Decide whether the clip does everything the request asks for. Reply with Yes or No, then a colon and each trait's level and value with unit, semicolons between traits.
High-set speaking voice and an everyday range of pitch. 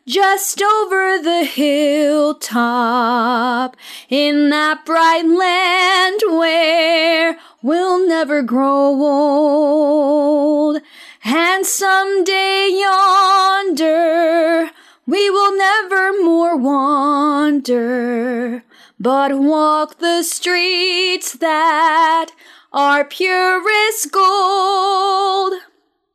Yes: very high, 330 Hz; average, 4.4 semitones